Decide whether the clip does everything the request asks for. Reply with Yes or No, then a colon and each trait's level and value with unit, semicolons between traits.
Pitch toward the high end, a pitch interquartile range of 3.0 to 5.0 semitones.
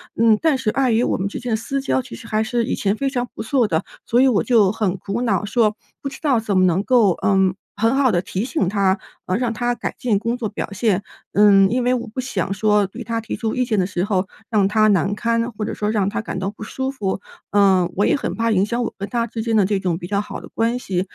Yes: high, 215 Hz; average, 3.5 semitones